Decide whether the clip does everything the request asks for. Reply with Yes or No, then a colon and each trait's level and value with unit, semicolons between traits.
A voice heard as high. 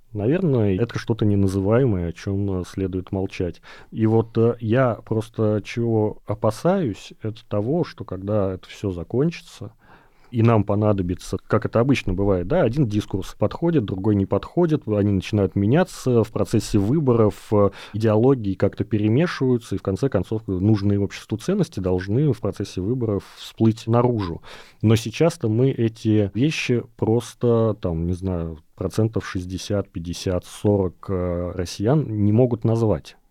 No: low, 105 Hz